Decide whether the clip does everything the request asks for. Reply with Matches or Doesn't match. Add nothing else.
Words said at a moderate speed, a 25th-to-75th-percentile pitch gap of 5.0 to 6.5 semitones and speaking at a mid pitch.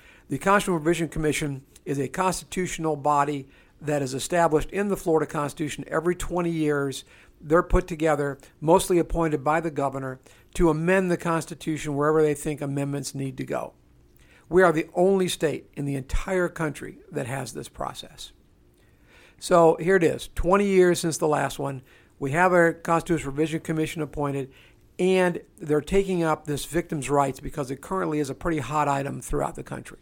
Doesn't match